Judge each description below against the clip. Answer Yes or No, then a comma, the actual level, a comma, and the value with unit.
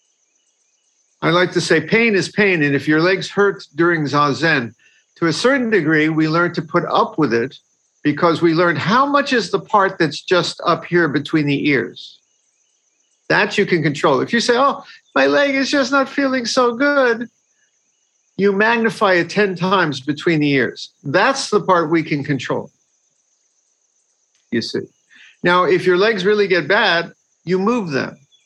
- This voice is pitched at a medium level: Yes, medium, 180 Hz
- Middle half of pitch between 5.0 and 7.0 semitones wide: Yes, average, 5.3 semitones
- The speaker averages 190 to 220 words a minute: No, average, 175 wpm